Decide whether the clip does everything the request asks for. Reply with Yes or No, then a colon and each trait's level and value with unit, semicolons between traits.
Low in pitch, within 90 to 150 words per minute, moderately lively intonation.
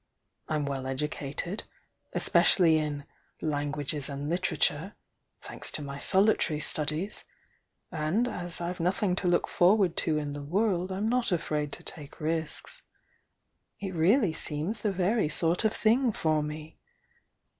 No: medium, 165 Hz; average, 140 wpm; average, 4.3 semitones